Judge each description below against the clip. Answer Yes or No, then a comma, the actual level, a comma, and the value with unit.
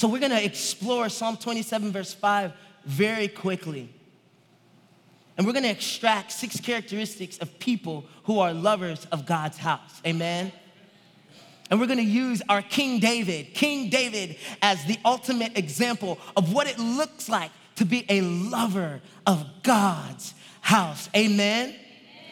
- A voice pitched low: No, high, 205 Hz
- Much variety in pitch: No, average, 4.1 semitones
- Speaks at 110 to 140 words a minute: Yes, slow, 135 wpm